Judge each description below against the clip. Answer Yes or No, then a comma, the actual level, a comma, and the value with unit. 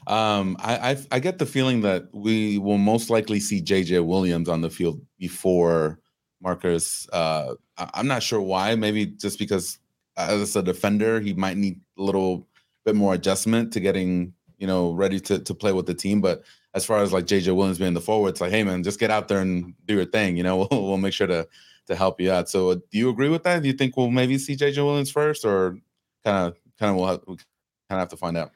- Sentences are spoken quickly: Yes, fast, 235 wpm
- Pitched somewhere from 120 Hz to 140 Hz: No, low, 100 Hz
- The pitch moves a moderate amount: Yes, average, 3.2 semitones